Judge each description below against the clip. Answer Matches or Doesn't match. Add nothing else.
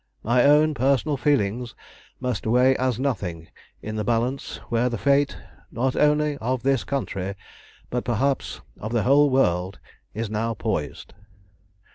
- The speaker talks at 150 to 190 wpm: Doesn't match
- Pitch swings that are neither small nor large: Matches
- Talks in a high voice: Doesn't match